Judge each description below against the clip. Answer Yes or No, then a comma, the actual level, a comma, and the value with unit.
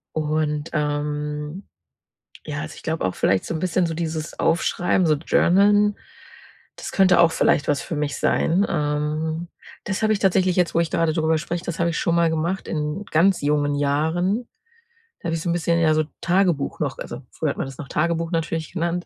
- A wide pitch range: No, narrow, 2.5 semitones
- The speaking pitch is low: No, medium, 165 Hz